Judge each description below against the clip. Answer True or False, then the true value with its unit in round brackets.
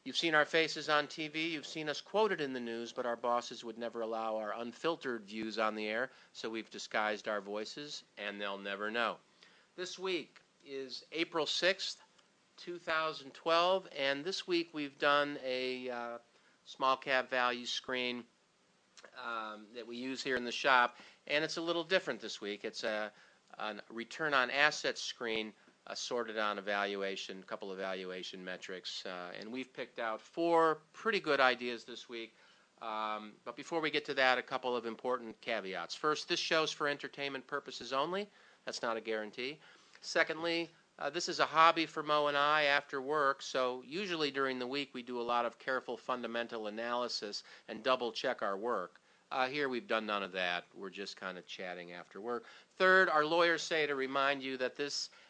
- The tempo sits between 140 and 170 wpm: False (180 wpm)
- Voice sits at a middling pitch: False (130 Hz)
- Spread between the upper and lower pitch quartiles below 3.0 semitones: False (5.2 semitones)